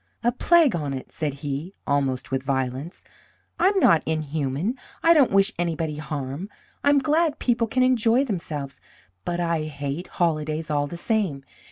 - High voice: No, medium, 165 Hz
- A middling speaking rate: Yes, average, 155 wpm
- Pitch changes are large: Yes, wide, 8.1 semitones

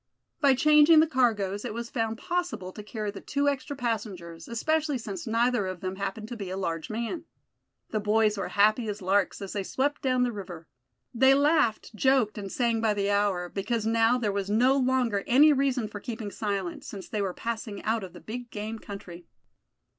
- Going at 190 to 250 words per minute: Yes, average, 200 wpm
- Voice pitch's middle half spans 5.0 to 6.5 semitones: No, average, 4.0 semitones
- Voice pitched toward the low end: No, high, 220 Hz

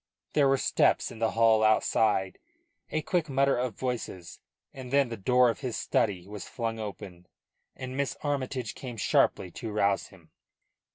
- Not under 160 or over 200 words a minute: Yes, average, 165 wpm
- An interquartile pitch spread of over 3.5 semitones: Yes, average, 3.9 semitones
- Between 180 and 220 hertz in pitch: No, low, 115 Hz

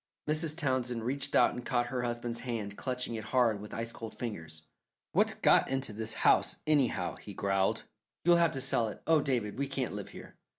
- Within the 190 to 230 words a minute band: Yes, average, 200 wpm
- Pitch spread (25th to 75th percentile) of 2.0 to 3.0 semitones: No, average, 3.7 semitones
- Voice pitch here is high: No, low, 120 Hz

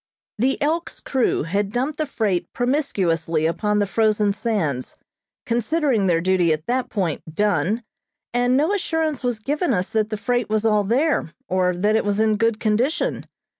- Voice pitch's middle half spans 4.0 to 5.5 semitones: Yes, average, 4.9 semitones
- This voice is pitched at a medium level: No, high, 215 Hz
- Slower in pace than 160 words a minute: No, average, 170 wpm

